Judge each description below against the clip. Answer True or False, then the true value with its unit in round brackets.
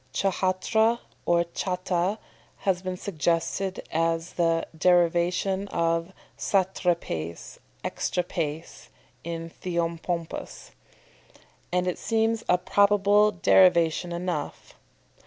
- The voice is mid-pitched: True (180 Hz)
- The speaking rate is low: True (85 wpm)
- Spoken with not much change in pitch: True (2.3 semitones)